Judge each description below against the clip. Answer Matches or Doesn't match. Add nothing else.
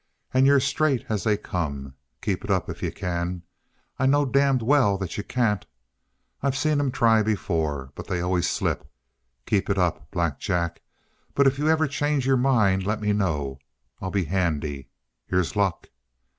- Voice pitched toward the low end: Matches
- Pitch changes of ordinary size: Doesn't match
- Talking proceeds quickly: Doesn't match